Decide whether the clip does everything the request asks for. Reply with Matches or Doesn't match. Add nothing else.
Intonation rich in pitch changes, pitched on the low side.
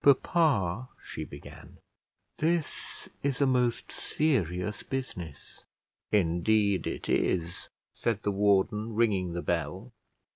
Matches